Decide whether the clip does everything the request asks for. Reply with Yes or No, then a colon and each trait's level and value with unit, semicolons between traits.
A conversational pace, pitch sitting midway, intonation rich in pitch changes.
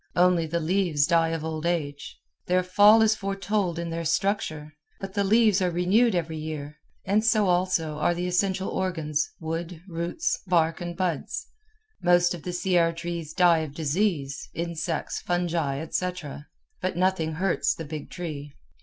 No: average, 155 wpm; medium, 175 Hz; average, 2.7 semitones